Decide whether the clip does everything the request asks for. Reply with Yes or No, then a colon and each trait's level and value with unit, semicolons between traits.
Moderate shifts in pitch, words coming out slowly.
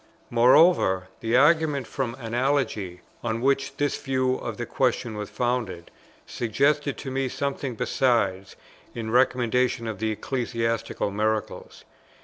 Yes: average, 3.4 semitones; slow, 125 wpm